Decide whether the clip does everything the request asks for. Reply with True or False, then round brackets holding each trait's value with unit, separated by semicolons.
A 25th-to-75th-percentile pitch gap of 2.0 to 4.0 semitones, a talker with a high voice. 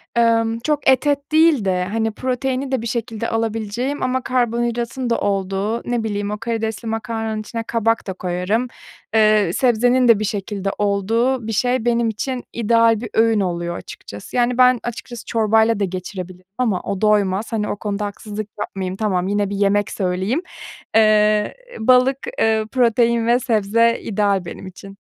True (2.8 semitones; 225 Hz)